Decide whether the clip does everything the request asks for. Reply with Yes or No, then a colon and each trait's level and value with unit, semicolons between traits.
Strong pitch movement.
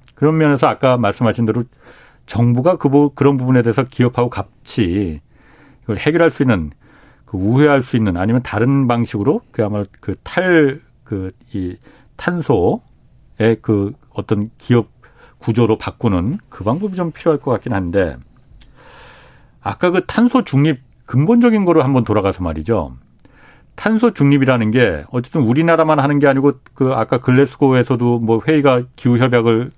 No: average, 4.3 semitones